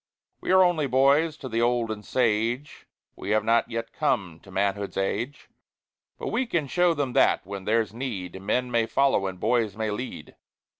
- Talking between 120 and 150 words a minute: No, average, 185 wpm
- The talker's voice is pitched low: Yes, low, 115 Hz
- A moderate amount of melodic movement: Yes, average, 4.6 semitones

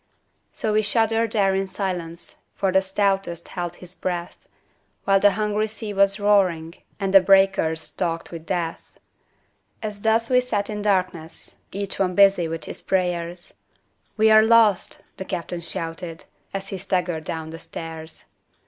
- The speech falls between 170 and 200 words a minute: No, average, 155 wpm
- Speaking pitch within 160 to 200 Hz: Yes, high, 190 Hz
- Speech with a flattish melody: No, average, 3.2 semitones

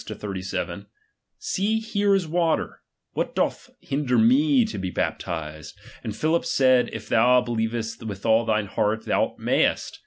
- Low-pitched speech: Yes, low, 120 Hz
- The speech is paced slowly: No, average, 155 wpm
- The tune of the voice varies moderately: No, wide, 8.4 semitones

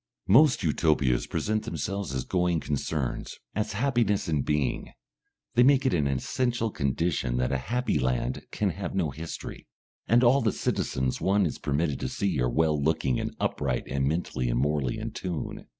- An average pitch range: No, wide, 7.3 semitones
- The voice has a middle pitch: No, very low, 80 Hz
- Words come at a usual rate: Yes, average, 170 wpm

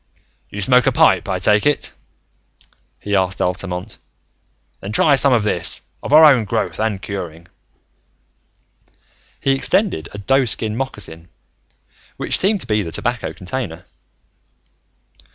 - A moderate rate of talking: No, slow, 130 wpm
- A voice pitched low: Yes, low, 105 Hz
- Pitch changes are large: Yes, wide, 6.1 semitones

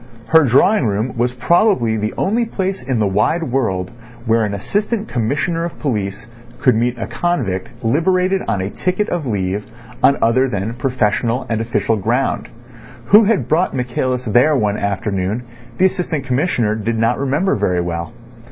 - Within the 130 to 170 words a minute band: Yes, average, 160 wpm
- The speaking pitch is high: No, low, 120 Hz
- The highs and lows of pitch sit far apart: Yes, wide, 7.2 semitones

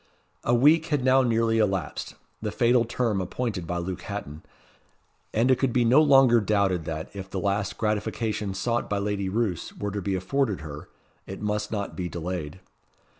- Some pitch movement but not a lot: Yes, average, 4.0 semitones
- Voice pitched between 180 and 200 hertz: No, low, 105 Hz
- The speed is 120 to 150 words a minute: No, average, 175 wpm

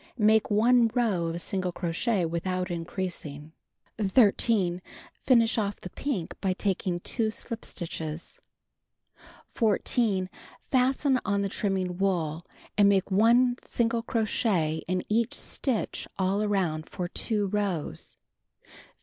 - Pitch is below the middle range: No, high, 195 Hz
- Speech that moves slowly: Yes, slow, 120 wpm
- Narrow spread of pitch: No, average, 4.2 semitones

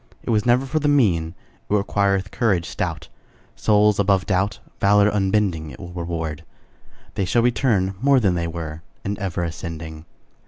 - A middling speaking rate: Yes, average, 160 wpm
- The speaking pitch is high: No, low, 100 Hz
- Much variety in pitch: No, average, 3.8 semitones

